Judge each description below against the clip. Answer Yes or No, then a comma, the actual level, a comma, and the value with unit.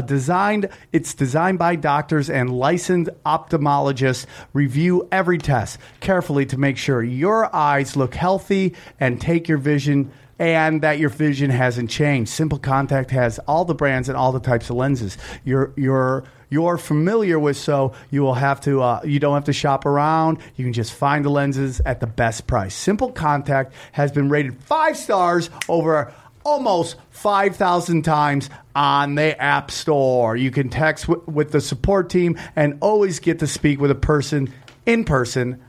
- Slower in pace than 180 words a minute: Yes, average, 170 wpm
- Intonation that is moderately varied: Yes, average, 3.6 semitones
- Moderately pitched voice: Yes, medium, 145 Hz